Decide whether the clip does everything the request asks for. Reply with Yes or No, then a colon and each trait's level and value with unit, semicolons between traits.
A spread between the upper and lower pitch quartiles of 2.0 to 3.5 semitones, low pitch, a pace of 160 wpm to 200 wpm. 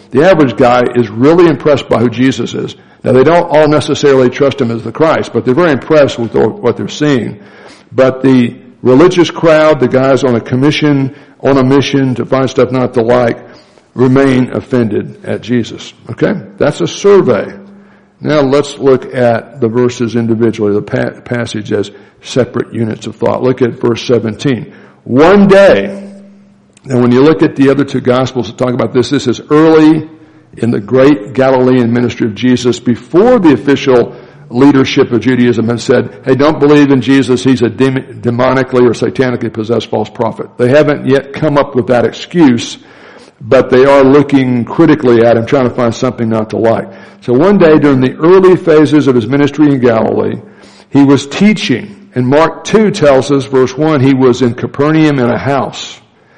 Yes: average, 3.2 semitones; low, 130 Hz; average, 180 wpm